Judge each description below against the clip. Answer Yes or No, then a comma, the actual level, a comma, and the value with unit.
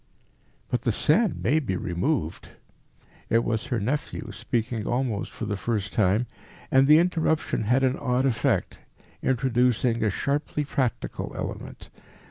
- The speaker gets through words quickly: No, slow, 135 wpm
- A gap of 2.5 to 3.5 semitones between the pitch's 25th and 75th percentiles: No, average, 4.0 semitones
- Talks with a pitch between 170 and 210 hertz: No, low, 120 Hz